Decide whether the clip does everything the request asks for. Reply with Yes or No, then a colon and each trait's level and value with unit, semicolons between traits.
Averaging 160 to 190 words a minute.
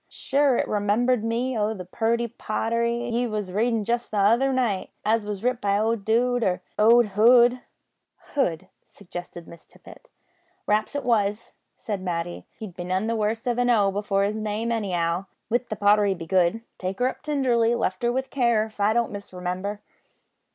Yes: average, 180 wpm